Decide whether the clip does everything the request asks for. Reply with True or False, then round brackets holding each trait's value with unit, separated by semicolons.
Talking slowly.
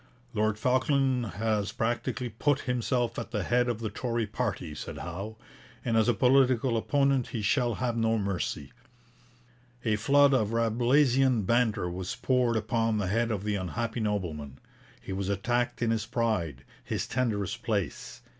False (155 wpm)